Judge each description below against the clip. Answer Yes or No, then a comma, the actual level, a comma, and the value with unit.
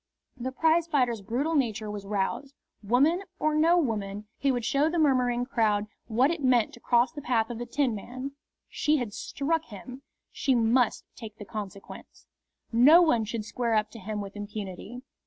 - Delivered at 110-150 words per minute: No, average, 175 wpm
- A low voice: No, high, 240 Hz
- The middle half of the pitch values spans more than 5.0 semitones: No, average, 4.6 semitones